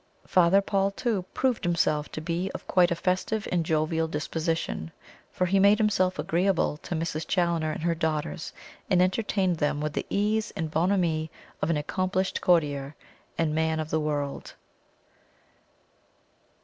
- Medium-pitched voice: Yes, medium, 170 Hz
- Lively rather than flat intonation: No, average, 3.1 semitones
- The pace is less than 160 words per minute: Yes, average, 150 wpm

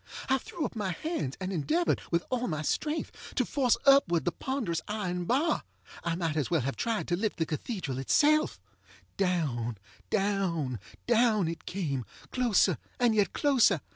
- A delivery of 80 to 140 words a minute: No, average, 165 wpm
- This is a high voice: Yes, high, 195 Hz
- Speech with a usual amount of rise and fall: No, wide, 7.2 semitones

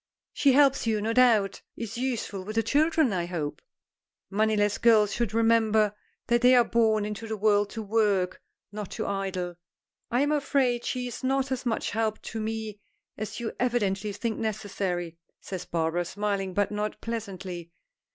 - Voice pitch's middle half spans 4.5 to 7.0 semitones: No, average, 3.0 semitones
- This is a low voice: No, high, 215 Hz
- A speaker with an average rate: Yes, average, 165 wpm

